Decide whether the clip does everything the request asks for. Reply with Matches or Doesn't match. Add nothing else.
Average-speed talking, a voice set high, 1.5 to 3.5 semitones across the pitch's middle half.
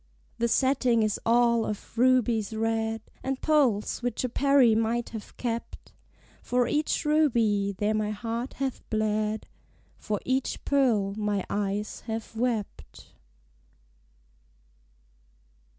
Doesn't match